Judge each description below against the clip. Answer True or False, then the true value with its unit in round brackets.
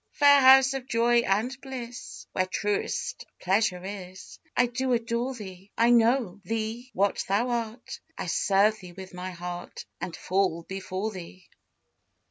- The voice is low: False (215 Hz)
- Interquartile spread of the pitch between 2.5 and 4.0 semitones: False (4.4 semitones)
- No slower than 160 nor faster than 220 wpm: False (145 wpm)